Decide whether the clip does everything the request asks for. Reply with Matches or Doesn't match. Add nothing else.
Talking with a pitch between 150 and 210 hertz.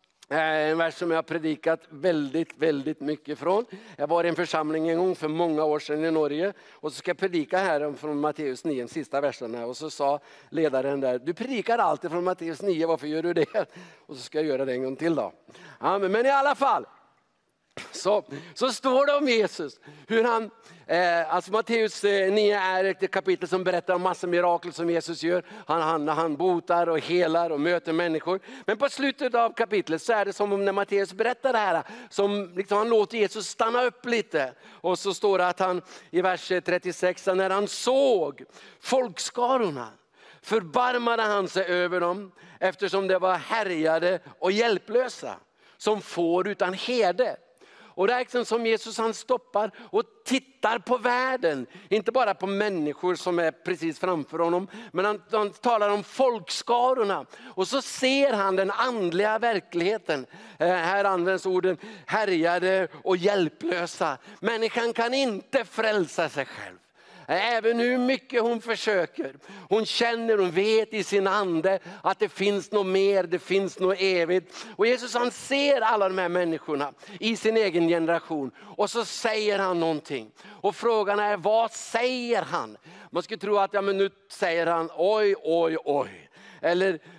Matches